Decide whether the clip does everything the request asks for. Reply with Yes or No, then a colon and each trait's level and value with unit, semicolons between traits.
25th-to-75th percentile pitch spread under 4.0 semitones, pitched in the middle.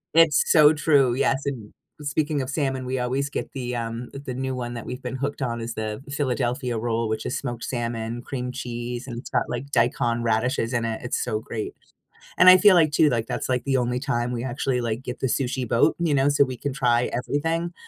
No: average, 2.8 semitones; low, 125 Hz